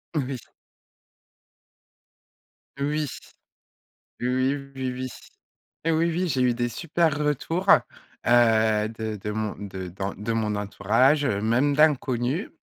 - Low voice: Yes, low, 125 Hz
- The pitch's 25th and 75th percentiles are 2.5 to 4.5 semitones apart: No, average, 5.1 semitones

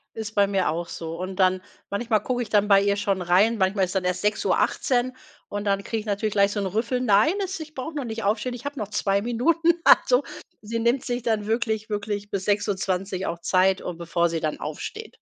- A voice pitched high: Yes, high, 205 Hz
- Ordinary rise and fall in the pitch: Yes, average, 3.5 semitones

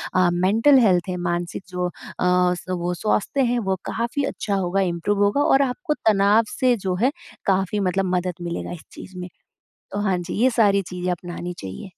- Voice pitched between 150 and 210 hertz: Yes, high, 190 Hz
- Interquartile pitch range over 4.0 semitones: No, average, 3.3 semitones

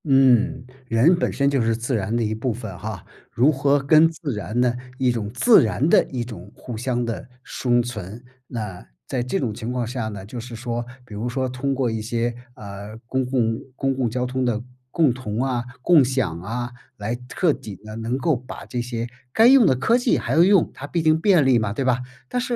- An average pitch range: Yes, average, 3.2 semitones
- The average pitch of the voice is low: Yes, low, 125 Hz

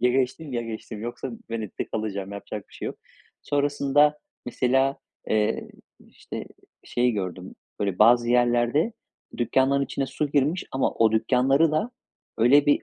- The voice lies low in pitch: Yes, low, 125 Hz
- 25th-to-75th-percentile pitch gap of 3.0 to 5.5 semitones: Yes, average, 3.9 semitones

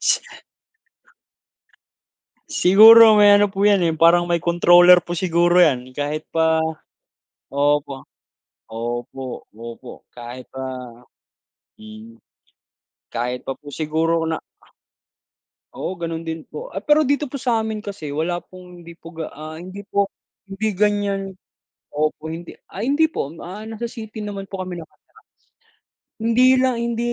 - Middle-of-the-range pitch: Yes, medium, 175 Hz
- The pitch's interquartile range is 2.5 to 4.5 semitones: No, average, 5.1 semitones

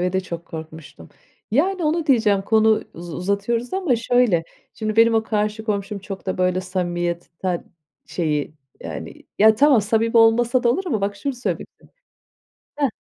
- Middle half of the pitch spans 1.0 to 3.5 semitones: No, average, 4.4 semitones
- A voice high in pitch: Yes, high, 215 Hz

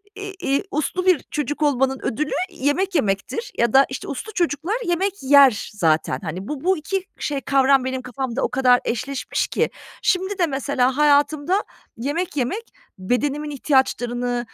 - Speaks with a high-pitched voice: Yes, very high, 280 Hz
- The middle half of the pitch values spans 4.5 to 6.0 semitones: Yes, average, 5.1 semitones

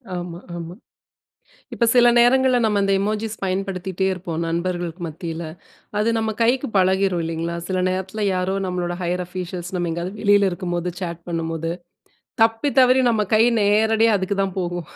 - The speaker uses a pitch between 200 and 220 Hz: No, medium, 185 Hz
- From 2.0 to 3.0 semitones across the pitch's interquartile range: No, average, 3.5 semitones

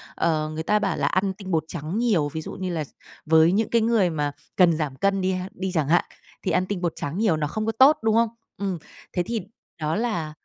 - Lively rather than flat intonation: No, average, 4.8 semitones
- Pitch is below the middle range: No, medium, 185 Hz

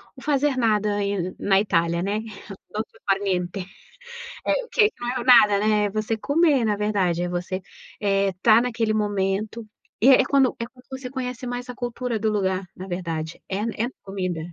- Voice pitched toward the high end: Yes, high, 210 Hz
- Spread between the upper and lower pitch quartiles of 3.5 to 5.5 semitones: Yes, average, 4.1 semitones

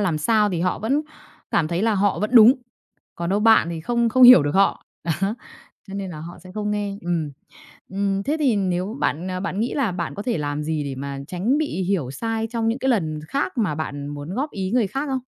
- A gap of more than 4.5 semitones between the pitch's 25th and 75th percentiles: Yes, average, 5.1 semitones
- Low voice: No, high, 195 Hz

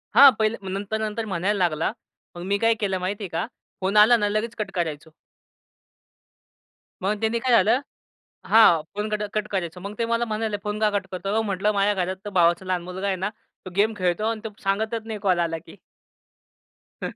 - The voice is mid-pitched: No, high, 205 Hz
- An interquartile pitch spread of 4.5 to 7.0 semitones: No, average, 2.8 semitones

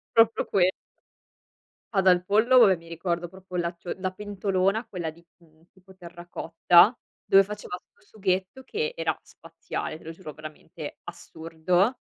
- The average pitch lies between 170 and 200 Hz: Yes, medium, 185 Hz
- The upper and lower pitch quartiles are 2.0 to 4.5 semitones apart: Yes, average, 2.7 semitones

